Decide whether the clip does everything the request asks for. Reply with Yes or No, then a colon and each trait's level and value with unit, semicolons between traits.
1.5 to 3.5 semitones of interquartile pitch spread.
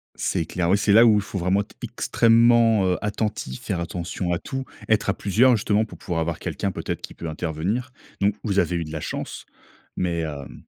No: average, 4.3 semitones